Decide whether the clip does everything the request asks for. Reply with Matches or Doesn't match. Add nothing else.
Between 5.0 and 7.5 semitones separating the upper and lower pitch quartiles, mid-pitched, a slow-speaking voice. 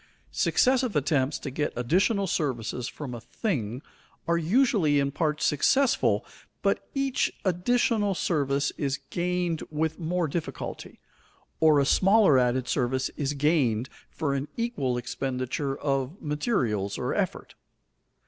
Matches